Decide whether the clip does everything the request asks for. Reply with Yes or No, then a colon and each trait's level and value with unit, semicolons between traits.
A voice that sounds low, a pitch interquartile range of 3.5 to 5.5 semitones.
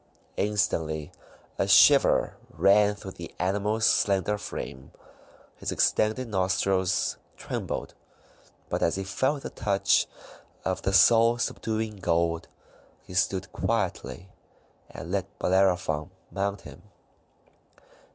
No: very low, 95 Hz; average, 2.7 semitones